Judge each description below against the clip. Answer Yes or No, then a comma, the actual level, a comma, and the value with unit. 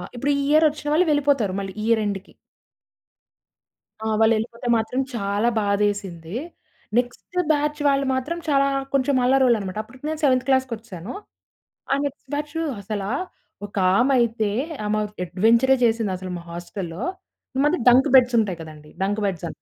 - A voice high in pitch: Yes, high, 230 Hz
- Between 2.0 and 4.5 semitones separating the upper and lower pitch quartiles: No, average, 5.1 semitones